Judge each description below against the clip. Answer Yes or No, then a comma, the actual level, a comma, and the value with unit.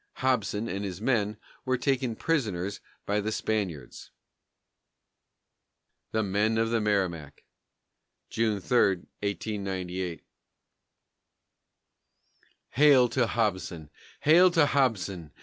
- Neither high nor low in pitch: No, low, 105 Hz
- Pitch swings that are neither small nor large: Yes, average, 4.5 semitones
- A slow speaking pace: Yes, slow, 95 wpm